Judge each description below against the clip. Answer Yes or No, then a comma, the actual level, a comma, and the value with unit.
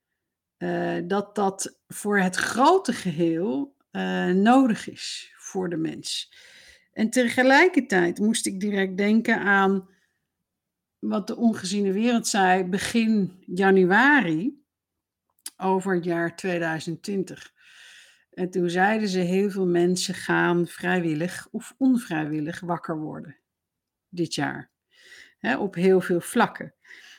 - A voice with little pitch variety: No, average, 3.8 semitones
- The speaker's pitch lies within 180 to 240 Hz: Yes, high, 190 Hz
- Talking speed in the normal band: No, slow, 115 wpm